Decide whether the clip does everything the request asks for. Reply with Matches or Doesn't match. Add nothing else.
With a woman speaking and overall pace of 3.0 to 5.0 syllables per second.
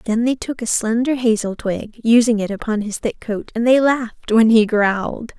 Matches